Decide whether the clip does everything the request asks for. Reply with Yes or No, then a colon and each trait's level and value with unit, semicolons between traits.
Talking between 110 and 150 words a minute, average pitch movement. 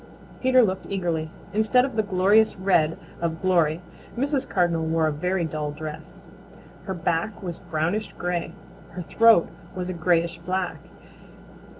Yes: average, 145 wpm; average, 3.3 semitones